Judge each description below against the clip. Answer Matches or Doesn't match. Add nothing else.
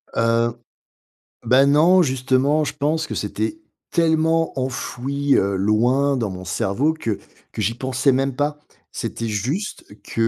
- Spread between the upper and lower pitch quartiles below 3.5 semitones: Doesn't match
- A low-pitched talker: Matches